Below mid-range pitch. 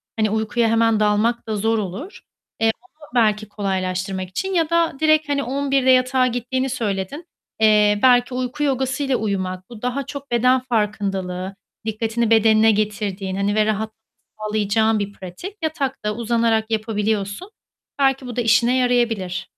No: high, 225 Hz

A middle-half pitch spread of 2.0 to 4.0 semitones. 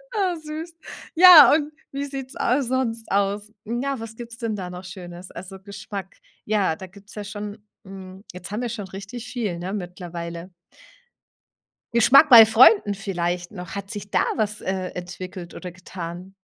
No: average, 4.4 semitones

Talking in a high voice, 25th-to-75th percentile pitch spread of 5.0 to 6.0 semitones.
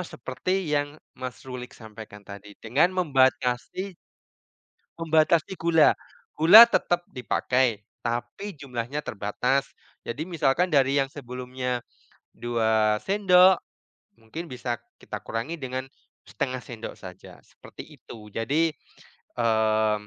No: low, 130 Hz; wide, 5.4 semitones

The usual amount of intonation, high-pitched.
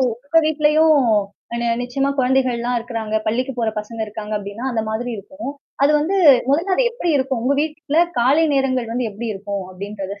Yes: average, 4.3 semitones; very high, 250 Hz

